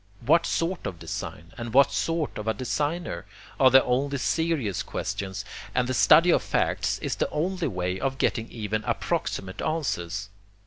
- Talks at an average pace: Yes, average, 165 wpm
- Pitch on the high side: No, low, 130 Hz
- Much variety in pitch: Yes, wide, 7.6 semitones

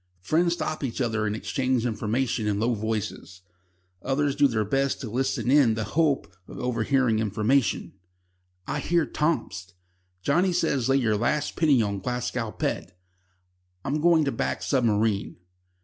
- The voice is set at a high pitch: No, low, 125 Hz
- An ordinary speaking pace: Yes, average, 150 wpm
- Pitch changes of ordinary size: Yes, average, 4.6 semitones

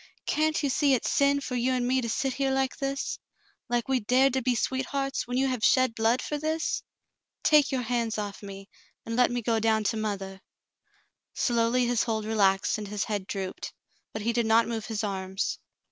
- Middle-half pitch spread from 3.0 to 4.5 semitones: Yes, average, 3.4 semitones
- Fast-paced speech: Yes, fast, 210 wpm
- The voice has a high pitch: Yes, high, 235 Hz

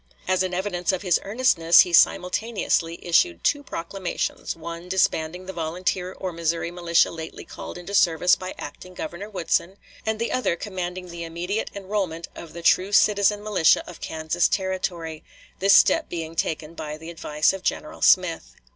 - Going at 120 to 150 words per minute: No, average, 165 wpm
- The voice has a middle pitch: Yes, medium, 175 Hz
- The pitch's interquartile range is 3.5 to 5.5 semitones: No, narrow, 2.5 semitones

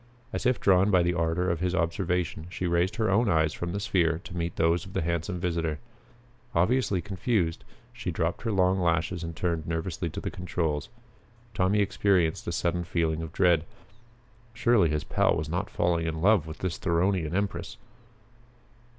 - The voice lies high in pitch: No, very low, 85 Hz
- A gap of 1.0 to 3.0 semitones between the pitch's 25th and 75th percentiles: Yes, narrow, 2.4 semitones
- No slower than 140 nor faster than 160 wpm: No, average, 175 wpm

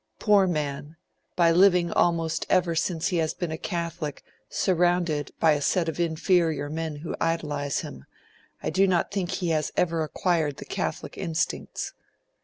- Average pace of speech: Yes, average, 160 wpm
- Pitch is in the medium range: Yes, medium, 165 Hz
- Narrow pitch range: Yes, narrow, 2.3 semitones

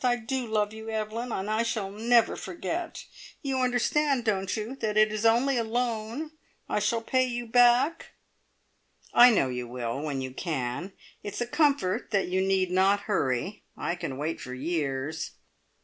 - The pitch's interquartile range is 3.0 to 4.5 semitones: No, average, 5.0 semitones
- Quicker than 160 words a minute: Yes, average, 170 wpm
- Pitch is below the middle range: No, high, 215 Hz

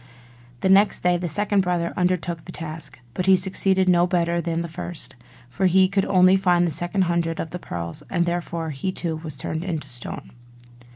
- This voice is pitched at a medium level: Yes, medium, 175 Hz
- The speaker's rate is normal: Yes, average, 195 wpm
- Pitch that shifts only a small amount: Yes, narrow, 2.1 semitones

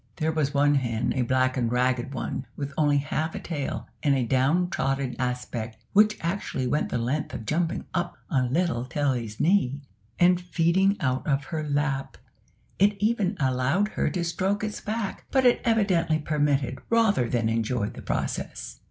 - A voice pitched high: No, medium, 145 Hz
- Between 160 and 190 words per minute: Yes, average, 170 wpm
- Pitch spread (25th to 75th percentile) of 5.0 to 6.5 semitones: Yes, wide, 5.6 semitones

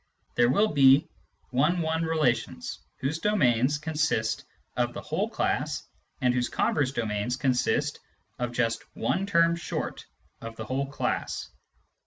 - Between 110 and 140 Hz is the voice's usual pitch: Yes, low, 135 Hz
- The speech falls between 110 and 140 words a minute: Yes, slow, 135 wpm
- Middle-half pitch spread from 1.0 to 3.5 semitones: No, average, 4.8 semitones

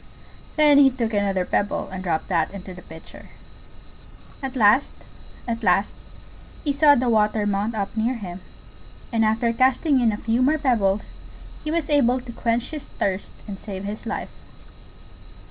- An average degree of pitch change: Yes, average, 4.5 semitones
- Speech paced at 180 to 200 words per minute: No, average, 165 wpm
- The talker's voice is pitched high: Yes, high, 225 Hz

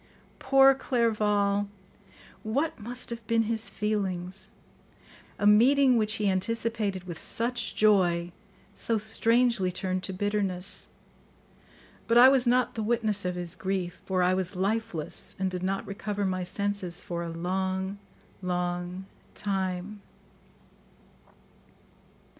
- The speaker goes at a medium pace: No, slow, 120 wpm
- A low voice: No, high, 200 Hz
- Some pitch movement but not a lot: Yes, average, 3.5 semitones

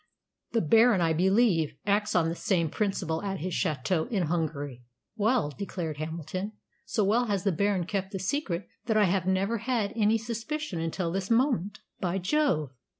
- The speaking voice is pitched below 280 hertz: Yes, high, 190 Hz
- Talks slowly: No, average, 170 wpm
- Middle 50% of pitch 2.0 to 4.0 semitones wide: No, average, 4.4 semitones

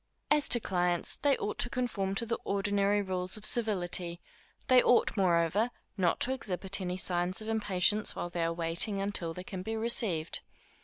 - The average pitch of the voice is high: Yes, high, 195 Hz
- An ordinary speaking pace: Yes, average, 175 wpm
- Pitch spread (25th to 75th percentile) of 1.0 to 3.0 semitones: No, average, 3.7 semitones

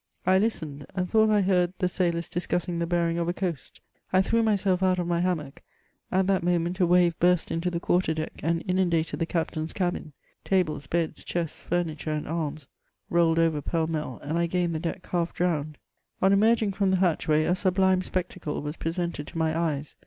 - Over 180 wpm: Yes, fast, 205 wpm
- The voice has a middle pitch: Yes, medium, 175 Hz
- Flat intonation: Yes, narrow, 2.3 semitones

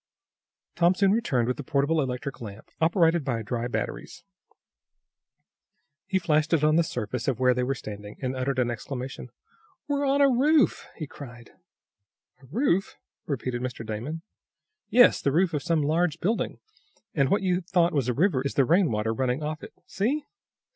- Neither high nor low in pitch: Yes, medium, 145 Hz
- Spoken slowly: No, average, 175 wpm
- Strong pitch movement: Yes, wide, 5.9 semitones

